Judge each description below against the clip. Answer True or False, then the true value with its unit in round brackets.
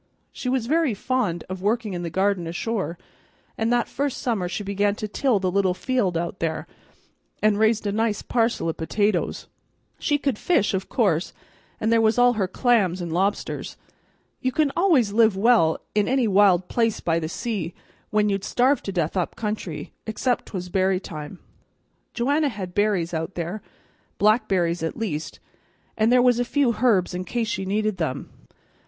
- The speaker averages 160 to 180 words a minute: True (175 wpm)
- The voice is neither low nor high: False (205 Hz)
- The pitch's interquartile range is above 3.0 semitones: True (4.6 semitones)